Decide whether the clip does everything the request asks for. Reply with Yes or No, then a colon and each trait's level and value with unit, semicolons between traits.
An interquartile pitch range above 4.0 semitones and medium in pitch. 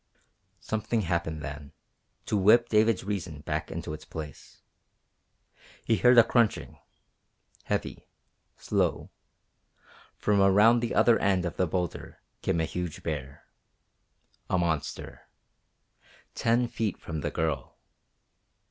No: wide, 5.5 semitones; very low, 90 Hz